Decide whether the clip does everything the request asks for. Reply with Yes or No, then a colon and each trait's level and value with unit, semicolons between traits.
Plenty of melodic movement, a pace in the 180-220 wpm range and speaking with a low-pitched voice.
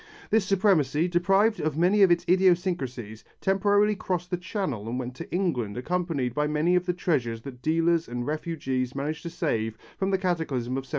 No: wide, 5.9 semitones; average, 185 wpm; medium, 165 Hz